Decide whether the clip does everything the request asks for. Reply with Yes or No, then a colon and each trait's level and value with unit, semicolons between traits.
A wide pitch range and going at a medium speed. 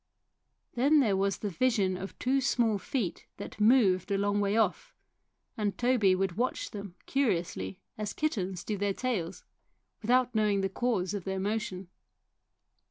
No: average, 3.9 semitones; average, 155 wpm